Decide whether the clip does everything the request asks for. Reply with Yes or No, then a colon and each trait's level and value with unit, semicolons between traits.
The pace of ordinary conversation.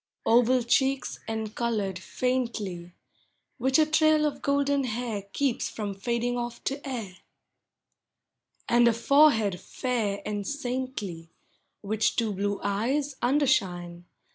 No: slow, 115 wpm